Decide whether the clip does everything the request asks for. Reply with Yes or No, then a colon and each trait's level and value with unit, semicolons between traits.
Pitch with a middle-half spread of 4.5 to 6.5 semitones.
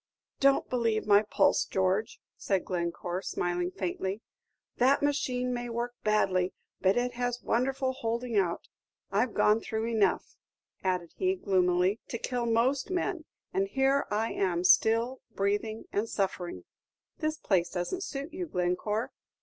Yes: average, 4.8 semitones